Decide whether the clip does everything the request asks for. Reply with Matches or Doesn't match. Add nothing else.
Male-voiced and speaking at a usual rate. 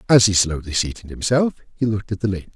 Doesn't match